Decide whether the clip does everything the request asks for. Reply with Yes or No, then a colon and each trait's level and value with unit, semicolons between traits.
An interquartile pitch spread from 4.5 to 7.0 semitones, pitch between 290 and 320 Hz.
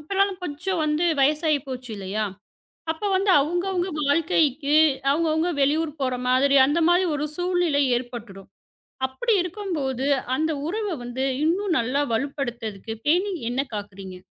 Yes: wide, 5.5 semitones; very high, 300 Hz